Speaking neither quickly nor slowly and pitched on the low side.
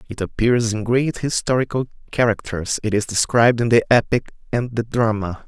Yes: average, 165 wpm; low, 115 Hz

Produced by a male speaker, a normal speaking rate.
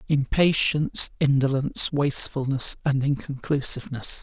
No: male; slow, 70 wpm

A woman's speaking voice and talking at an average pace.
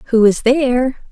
Yes: female; average, 160 wpm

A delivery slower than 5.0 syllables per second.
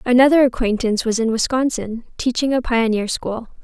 No: 5.5 syllables/s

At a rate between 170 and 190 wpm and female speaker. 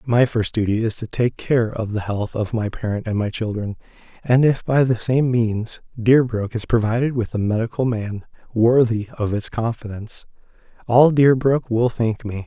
No: average, 185 wpm; male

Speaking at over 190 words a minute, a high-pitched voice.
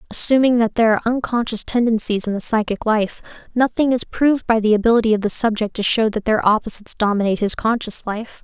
Yes: average, 200 wpm; high, 225 Hz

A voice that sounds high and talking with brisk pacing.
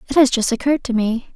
Yes: high, 245 Hz; fast, 265 wpm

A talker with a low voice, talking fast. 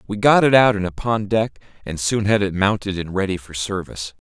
Yes: low, 100 Hz; fast, 225 wpm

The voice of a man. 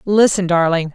No: female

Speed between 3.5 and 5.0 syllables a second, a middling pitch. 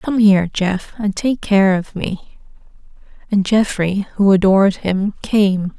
No: 3.8 syllables/s; high, 200 Hz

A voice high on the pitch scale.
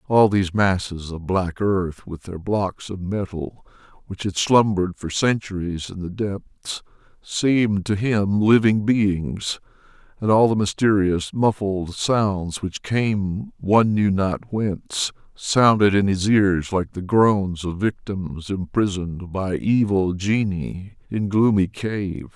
No: low, 100 Hz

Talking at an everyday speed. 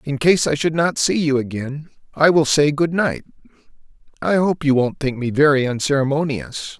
Yes: average, 185 wpm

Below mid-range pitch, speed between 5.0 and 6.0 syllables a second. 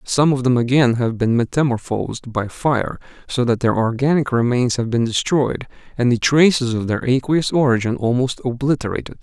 Yes: low, 125 Hz; 5.2 syllables/s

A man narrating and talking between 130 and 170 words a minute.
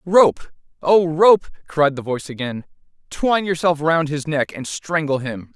Yes: male; average, 160 wpm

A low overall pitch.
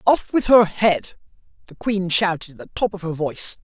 No: high, 190 Hz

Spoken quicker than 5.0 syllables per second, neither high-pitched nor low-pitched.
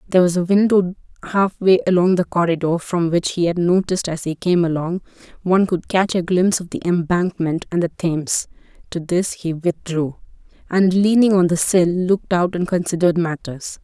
Yes: 5.3 syllables/s; medium, 175 Hz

